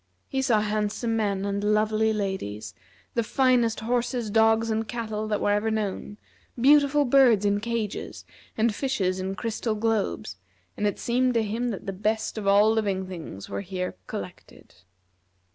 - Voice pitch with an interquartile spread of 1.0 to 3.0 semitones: Yes, narrow, 2.5 semitones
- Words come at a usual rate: Yes, average, 160 wpm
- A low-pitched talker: No, high, 215 Hz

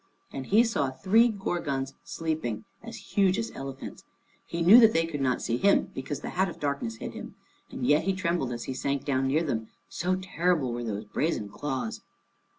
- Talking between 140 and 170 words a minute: No, average, 195 wpm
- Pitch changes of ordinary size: No, wide, 6.1 semitones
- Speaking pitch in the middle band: Yes, medium, 150 Hz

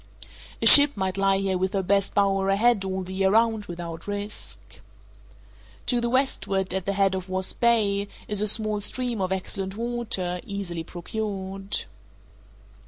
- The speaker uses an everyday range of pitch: No, narrow, 2.1 semitones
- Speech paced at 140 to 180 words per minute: Yes, average, 160 wpm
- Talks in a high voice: Yes, high, 195 Hz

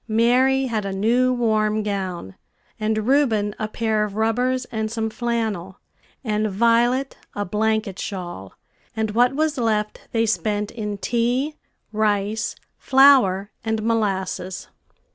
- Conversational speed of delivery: No, slow, 125 wpm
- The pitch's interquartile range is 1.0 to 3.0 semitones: Yes, narrow, 2.4 semitones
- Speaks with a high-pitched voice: Yes, high, 220 Hz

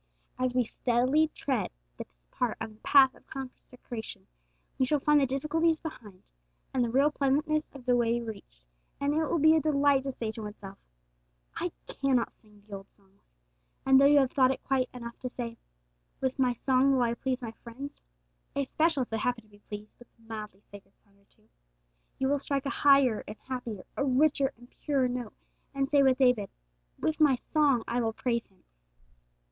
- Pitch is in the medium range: No, very high, 255 Hz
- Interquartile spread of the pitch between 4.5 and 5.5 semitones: No, average, 3.5 semitones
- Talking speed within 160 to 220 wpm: Yes, average, 195 wpm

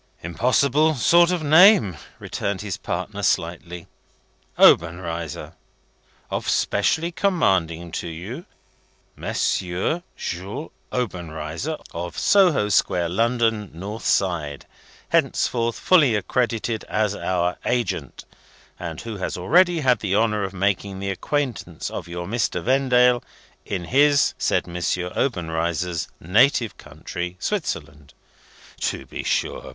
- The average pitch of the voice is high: No, low, 100 Hz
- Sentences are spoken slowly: Yes, slow, 115 wpm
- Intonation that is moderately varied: No, wide, 6.4 semitones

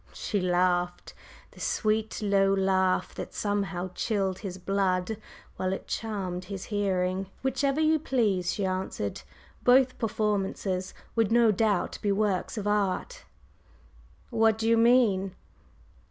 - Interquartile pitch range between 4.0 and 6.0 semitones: No, average, 3.1 semitones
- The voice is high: Yes, high, 200 Hz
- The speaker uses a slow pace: Yes, slow, 125 wpm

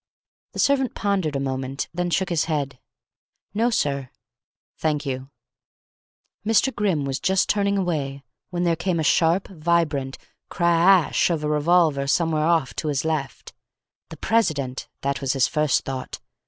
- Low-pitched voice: No, medium, 160 Hz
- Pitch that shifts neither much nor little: Yes, average, 4.4 semitones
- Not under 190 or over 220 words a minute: No, average, 155 wpm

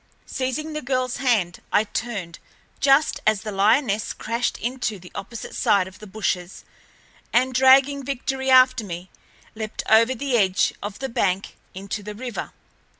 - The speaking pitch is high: Yes, high, 230 Hz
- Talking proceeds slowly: No, average, 150 wpm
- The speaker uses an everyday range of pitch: Yes, average, 4.6 semitones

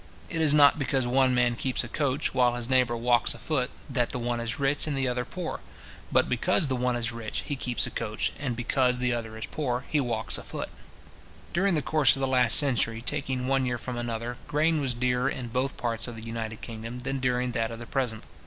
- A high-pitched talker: No, low, 125 Hz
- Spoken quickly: Yes, fast, 235 wpm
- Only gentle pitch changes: Yes, narrow, 2.3 semitones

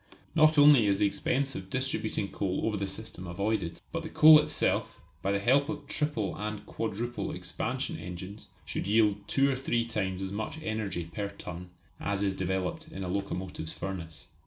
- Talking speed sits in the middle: Yes, average, 180 wpm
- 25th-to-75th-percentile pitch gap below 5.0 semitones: No, average, 5.3 semitones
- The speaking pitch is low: Yes, low, 105 Hz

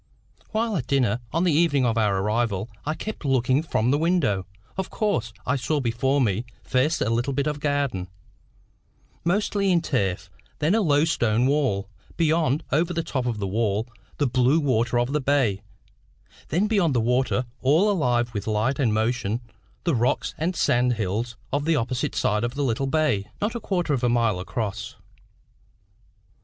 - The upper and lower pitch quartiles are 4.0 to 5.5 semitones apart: Yes, average, 5.2 semitones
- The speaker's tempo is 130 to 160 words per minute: No, average, 180 wpm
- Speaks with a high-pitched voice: No, low, 130 Hz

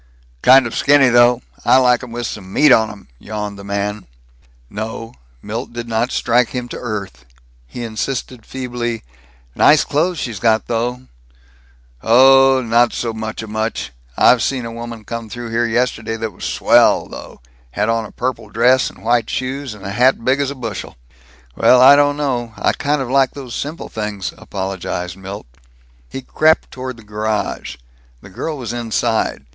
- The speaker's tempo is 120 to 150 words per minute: No, average, 170 wpm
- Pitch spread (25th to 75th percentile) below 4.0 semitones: Yes, average, 2.8 semitones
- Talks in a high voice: No, low, 120 Hz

